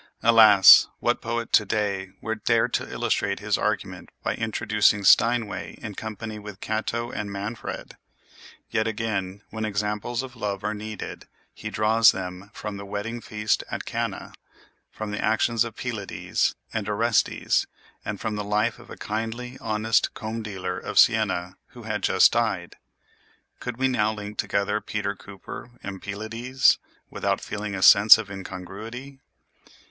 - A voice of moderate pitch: No, low, 105 Hz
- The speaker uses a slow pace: No, average, 150 wpm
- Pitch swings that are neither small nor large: No, narrow, 1.9 semitones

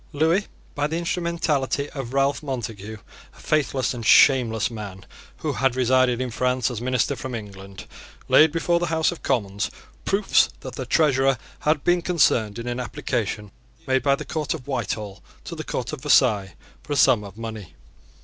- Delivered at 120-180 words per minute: Yes, average, 175 wpm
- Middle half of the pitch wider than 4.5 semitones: Yes, average, 5.0 semitones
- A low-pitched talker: Yes, low, 130 Hz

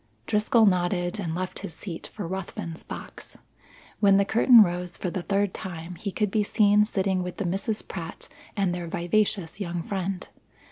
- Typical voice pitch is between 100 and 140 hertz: No, high, 190 Hz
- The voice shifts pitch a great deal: No, narrow, 2.6 semitones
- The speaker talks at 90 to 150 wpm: No, average, 175 wpm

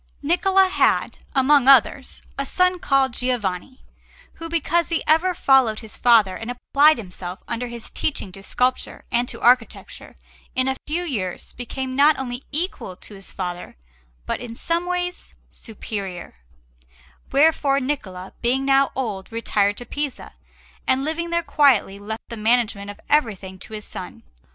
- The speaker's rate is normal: Yes, average, 150 wpm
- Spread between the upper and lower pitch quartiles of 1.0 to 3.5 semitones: No, wide, 5.6 semitones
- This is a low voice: No, very high, 255 Hz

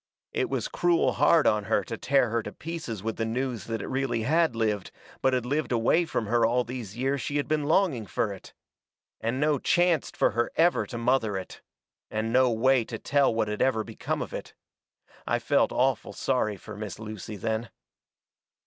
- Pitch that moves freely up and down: No, average, 3.7 semitones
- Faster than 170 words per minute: Yes, average, 200 wpm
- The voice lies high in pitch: No, low, 120 Hz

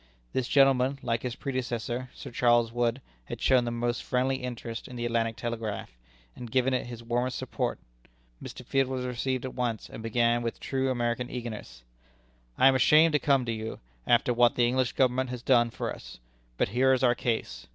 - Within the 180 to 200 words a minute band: Yes, average, 195 wpm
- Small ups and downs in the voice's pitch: Yes, narrow, 1.6 semitones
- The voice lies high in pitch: No, low, 120 Hz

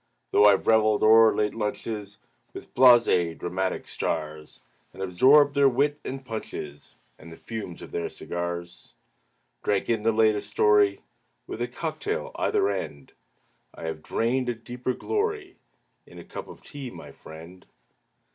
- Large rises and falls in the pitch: Yes, wide, 6.0 semitones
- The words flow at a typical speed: Yes, average, 150 wpm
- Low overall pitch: Yes, low, 110 Hz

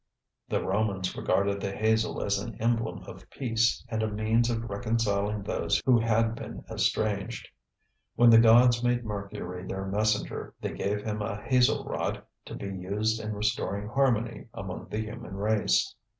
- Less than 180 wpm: Yes, average, 160 wpm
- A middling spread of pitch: No, narrow, 2.2 semitones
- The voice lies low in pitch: Yes, low, 110 Hz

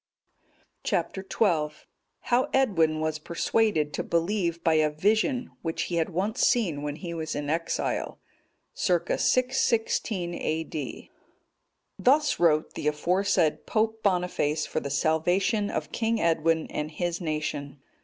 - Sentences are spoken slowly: Yes, slow, 130 wpm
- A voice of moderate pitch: Yes, medium, 170 Hz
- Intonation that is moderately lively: Yes, average, 4.9 semitones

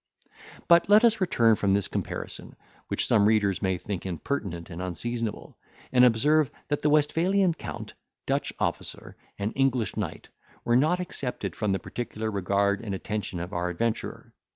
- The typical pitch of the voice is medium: No, low, 110 Hz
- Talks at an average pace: Yes, average, 155 wpm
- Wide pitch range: Yes, wide, 6.5 semitones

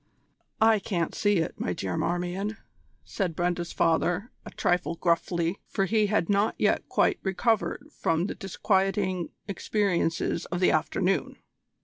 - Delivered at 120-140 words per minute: Yes, slow, 135 wpm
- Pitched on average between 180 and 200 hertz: Yes, medium, 185 Hz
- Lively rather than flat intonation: No, average, 3.0 semitones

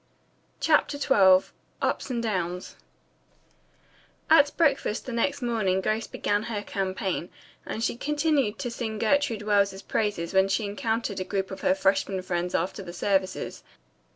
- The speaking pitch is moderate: No, high, 210 Hz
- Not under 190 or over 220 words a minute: No, average, 145 wpm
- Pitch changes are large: No, average, 3.9 semitones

